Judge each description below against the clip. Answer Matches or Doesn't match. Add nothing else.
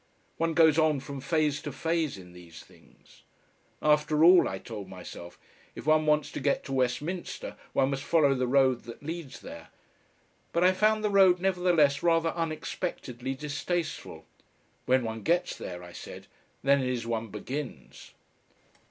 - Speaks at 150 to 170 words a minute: Matches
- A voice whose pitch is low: Doesn't match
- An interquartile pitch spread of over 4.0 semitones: Matches